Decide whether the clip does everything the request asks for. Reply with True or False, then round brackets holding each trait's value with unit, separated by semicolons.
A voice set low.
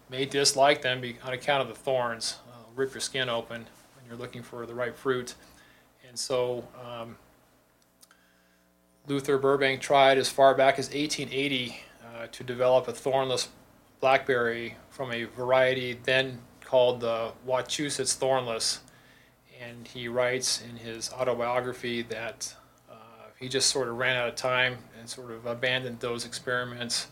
True (125 Hz)